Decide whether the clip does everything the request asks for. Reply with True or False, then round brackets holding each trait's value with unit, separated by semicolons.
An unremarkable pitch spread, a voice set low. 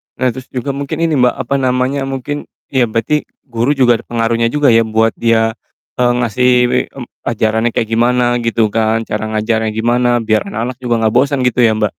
False (2.3 semitones; 120 Hz)